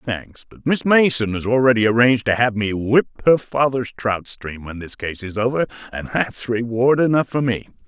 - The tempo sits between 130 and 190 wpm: No, average, 200 wpm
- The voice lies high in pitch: No, low, 120 Hz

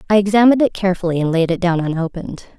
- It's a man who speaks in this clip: No, female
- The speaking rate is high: Yes, fast, 210 wpm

